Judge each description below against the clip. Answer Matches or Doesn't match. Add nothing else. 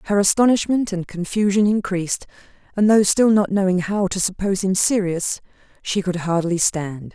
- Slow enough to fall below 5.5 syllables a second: Matches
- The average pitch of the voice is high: Matches